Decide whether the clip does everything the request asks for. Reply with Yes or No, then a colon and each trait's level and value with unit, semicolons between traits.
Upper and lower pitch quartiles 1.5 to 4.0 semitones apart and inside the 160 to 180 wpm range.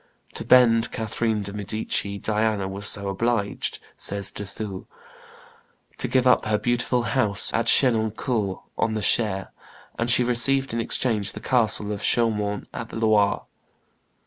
No: narrow, 2.6 semitones; average, 145 wpm